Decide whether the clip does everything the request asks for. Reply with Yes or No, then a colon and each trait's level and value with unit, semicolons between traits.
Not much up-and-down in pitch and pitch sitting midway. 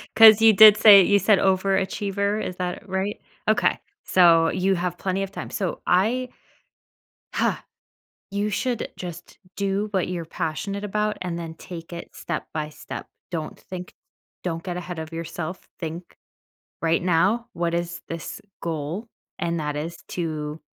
No: average, 3.2 semitones; medium, 180 Hz